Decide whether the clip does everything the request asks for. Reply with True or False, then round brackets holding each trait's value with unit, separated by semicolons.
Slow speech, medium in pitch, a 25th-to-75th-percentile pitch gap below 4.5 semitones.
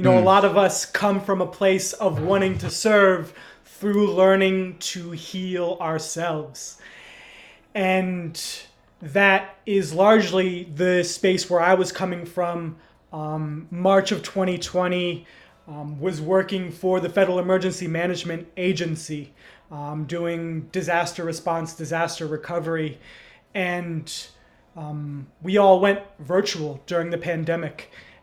True (125 wpm; 175 Hz; 2.5 semitones)